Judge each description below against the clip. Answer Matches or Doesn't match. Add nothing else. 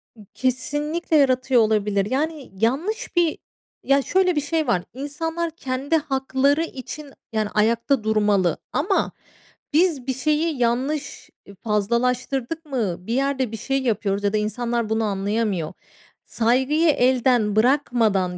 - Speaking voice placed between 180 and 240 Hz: Doesn't match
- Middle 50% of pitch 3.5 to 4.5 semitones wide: Doesn't match